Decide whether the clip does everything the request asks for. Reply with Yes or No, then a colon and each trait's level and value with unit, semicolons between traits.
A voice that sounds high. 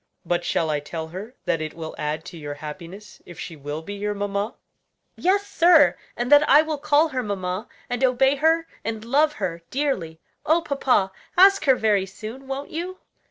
Yes: high, 220 Hz